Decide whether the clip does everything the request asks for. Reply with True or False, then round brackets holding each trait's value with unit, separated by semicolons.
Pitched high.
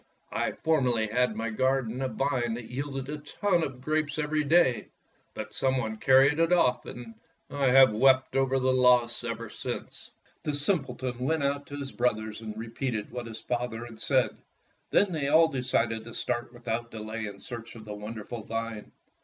False (125 Hz)